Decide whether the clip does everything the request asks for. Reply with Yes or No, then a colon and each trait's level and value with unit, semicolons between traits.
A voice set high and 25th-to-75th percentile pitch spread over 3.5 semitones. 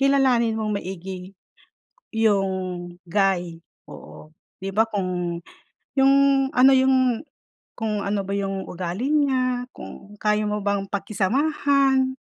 Yes: high, 210 Hz; average, 5.3 semitones